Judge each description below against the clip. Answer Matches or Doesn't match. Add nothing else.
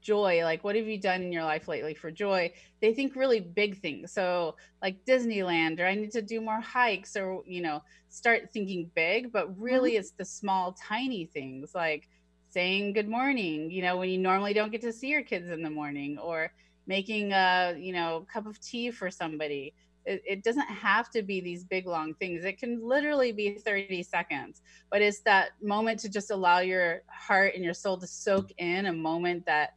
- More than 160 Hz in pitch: Matches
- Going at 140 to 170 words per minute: Doesn't match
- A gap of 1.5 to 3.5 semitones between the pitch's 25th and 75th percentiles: Doesn't match